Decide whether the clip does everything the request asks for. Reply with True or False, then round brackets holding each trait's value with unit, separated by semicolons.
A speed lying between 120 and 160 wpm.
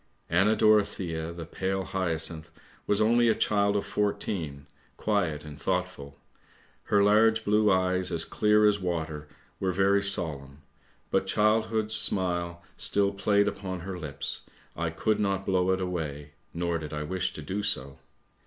True (155 wpm)